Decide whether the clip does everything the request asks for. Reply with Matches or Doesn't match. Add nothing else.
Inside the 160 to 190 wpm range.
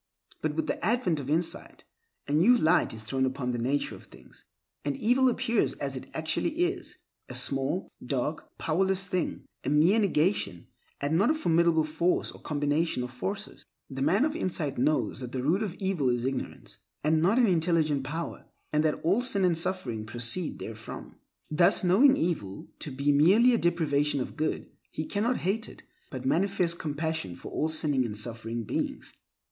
Matches